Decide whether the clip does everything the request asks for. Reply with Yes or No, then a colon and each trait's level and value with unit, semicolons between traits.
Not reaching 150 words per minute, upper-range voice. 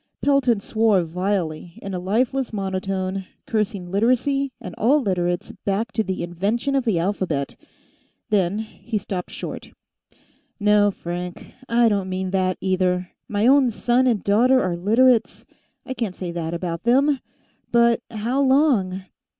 Yes: average, 140 wpm; high, 205 Hz